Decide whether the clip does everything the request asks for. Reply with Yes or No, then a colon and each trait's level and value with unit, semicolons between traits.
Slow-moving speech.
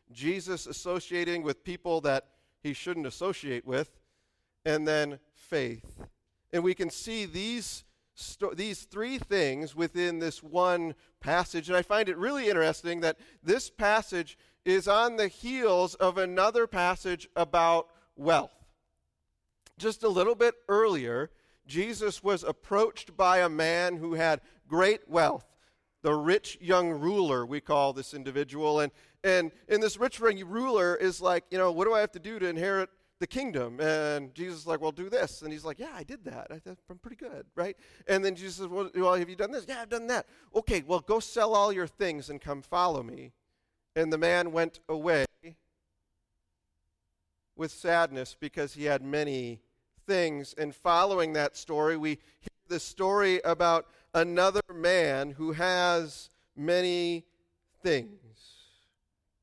No: average, 155 wpm